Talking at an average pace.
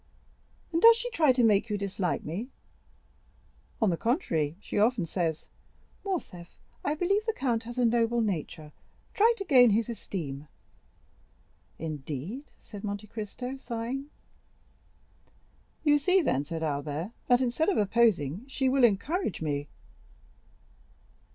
No: slow, 130 wpm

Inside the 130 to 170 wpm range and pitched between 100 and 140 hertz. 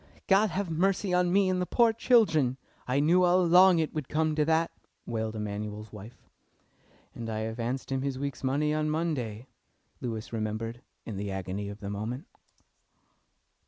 Yes: average, 165 wpm; low, 135 Hz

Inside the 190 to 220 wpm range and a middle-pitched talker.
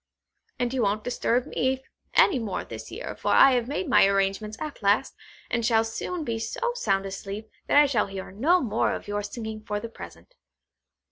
No: average, 195 wpm; high, 225 Hz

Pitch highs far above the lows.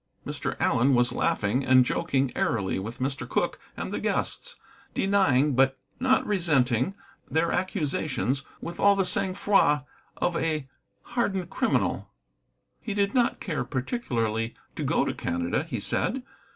Yes: wide, 7.6 semitones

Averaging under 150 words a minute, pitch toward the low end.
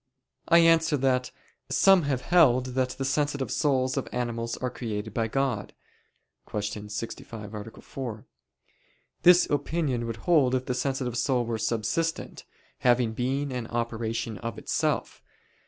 Yes: average, 140 wpm; low, 125 Hz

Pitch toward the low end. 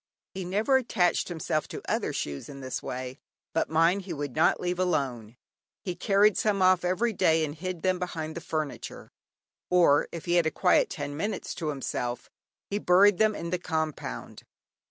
No: medium, 170 Hz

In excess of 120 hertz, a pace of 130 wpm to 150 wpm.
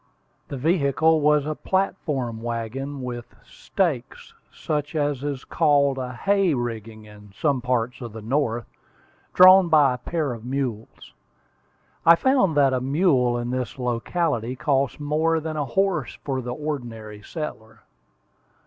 Yes: low, 135 Hz; average, 140 wpm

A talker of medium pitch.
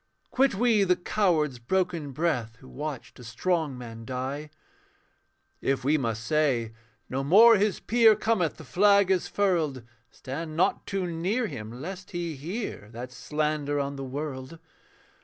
Yes: medium, 155 Hz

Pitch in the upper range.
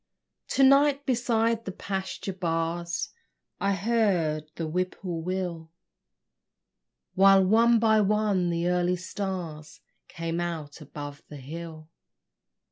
No: medium, 180 Hz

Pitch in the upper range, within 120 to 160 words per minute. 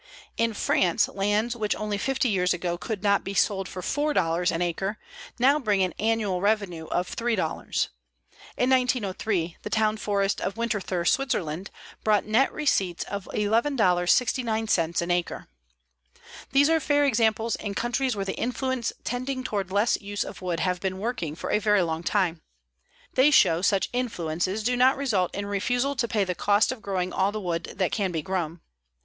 No: high, 205 Hz; average, 170 wpm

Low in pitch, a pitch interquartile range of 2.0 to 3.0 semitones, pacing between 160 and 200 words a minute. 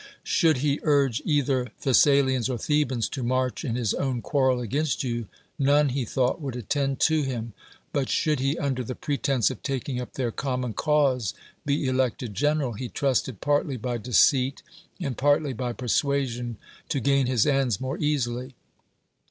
Yes: low, 130 Hz; narrow, 2.5 semitones; average, 170 wpm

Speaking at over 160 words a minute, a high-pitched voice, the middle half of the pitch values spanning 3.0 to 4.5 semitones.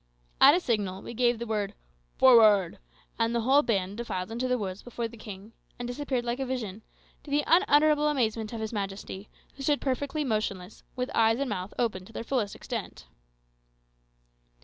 Yes: average, 180 wpm; high, 230 Hz; average, 4.0 semitones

